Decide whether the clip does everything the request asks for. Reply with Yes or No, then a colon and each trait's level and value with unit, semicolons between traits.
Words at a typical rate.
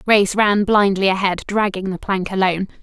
Yes: average, 170 wpm